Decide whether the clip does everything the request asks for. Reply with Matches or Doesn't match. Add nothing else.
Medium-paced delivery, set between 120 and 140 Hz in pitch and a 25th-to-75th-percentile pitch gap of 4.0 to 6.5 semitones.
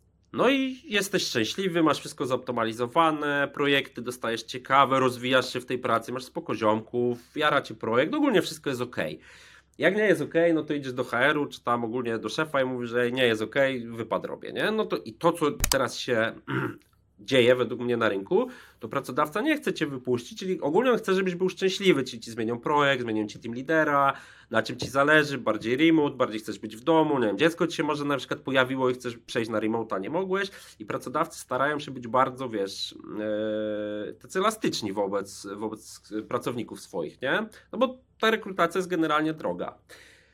Doesn't match